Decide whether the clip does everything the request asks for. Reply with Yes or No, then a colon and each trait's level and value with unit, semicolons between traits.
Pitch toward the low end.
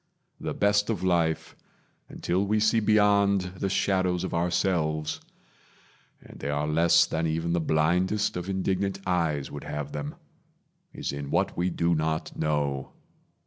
Yes: very low, 85 Hz